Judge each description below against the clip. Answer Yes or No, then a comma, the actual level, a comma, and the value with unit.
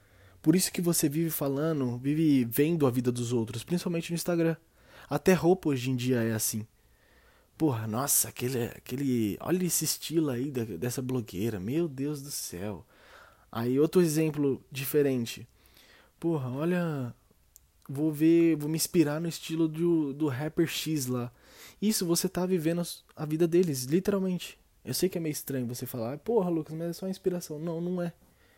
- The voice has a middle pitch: Yes, medium, 150 Hz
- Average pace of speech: Yes, average, 170 wpm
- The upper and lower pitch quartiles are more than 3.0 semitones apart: Yes, average, 5.1 semitones